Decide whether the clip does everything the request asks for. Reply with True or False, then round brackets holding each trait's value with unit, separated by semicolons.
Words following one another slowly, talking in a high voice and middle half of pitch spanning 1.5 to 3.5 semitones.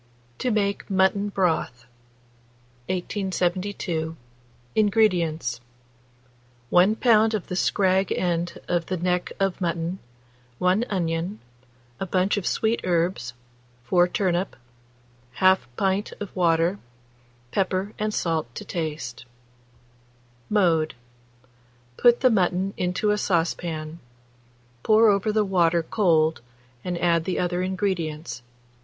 False (110 wpm; 180 Hz; 3.1 semitones)